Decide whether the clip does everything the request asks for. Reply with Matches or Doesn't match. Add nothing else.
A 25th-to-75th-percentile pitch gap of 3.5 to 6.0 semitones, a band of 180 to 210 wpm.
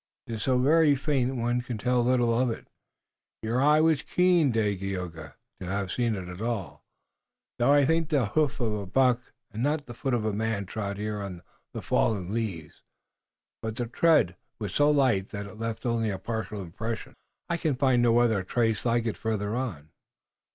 Matches